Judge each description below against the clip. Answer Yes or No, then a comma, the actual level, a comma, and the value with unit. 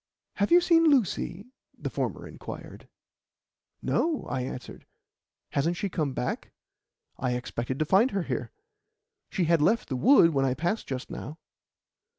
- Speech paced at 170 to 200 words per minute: No, average, 150 wpm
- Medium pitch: Yes, medium, 165 Hz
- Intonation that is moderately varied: No, wide, 8.5 semitones